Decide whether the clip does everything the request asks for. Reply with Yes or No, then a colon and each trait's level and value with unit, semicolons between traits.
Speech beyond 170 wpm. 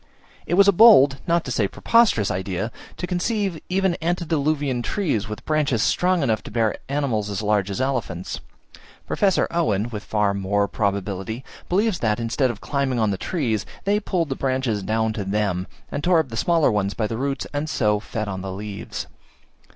Yes: average, 185 wpm